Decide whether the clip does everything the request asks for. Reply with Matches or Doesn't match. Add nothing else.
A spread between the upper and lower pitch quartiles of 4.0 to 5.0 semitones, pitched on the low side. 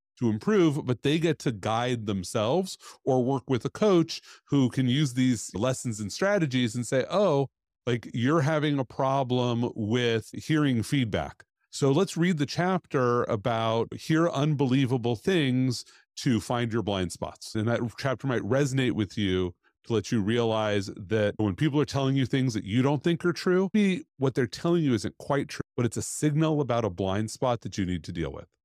Matches